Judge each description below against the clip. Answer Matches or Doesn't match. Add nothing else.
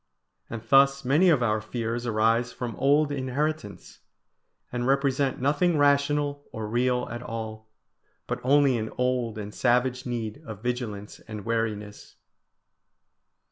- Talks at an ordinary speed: Doesn't match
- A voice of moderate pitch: Doesn't match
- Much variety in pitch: Doesn't match